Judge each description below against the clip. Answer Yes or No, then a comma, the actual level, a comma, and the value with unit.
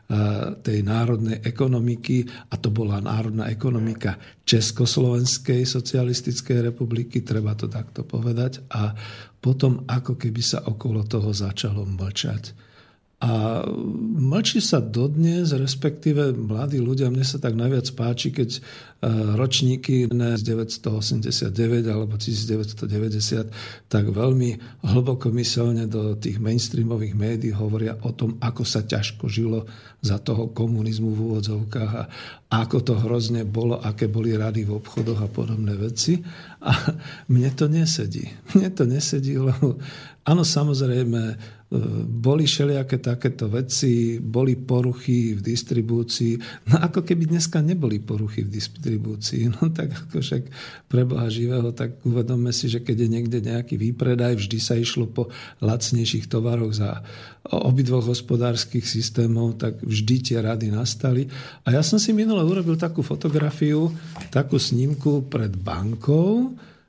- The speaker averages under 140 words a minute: Yes, average, 130 wpm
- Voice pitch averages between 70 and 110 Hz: No, low, 120 Hz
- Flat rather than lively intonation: No, average, 3.0 semitones